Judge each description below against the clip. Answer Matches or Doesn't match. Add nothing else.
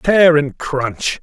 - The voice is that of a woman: Doesn't match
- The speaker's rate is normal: Matches